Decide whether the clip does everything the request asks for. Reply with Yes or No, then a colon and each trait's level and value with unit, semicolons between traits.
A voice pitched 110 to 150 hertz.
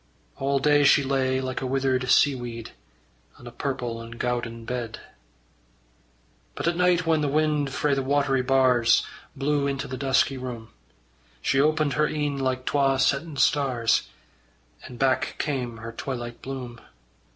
Yes: low, 135 Hz